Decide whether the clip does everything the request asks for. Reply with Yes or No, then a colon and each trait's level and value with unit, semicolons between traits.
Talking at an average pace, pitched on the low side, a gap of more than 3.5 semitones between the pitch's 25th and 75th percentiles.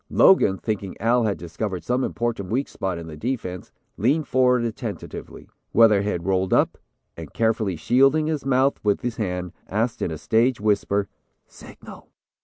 Yes: average, 155 wpm; low, 110 Hz; average, 4.9 semitones